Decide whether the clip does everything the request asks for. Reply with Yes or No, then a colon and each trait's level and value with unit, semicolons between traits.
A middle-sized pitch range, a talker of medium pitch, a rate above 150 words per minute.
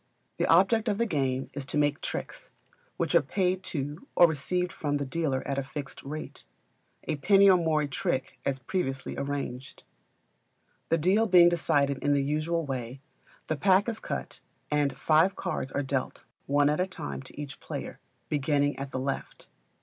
Yes: average, 4.2 semitones; medium, 150 Hz; average, 180 wpm